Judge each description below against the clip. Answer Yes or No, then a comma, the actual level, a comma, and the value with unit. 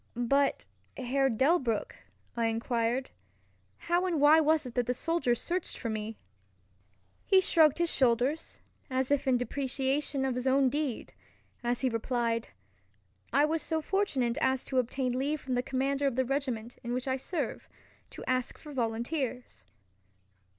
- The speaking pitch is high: Yes, very high, 260 Hz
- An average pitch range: Yes, average, 3.1 semitones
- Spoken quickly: No, average, 155 wpm